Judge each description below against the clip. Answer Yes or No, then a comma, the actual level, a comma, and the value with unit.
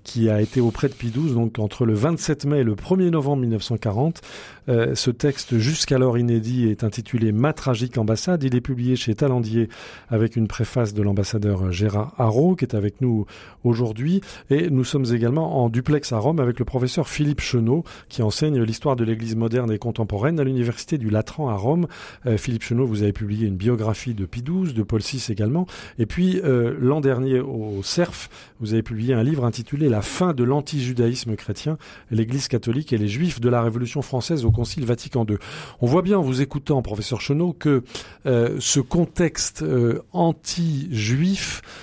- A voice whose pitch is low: Yes, low, 125 Hz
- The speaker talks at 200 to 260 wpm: No, average, 185 wpm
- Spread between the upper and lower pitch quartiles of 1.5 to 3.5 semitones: No, average, 4.3 semitones